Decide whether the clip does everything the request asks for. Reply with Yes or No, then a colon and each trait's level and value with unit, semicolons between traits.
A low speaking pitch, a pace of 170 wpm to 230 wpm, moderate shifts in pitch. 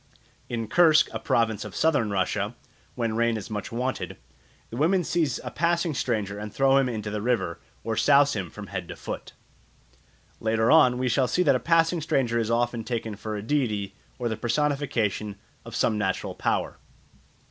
Yes: low, 115 Hz; average, 180 wpm; average, 4.5 semitones